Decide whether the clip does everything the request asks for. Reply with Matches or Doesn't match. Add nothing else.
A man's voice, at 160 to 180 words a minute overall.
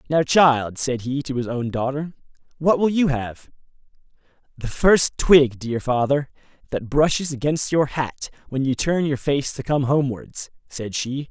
Matches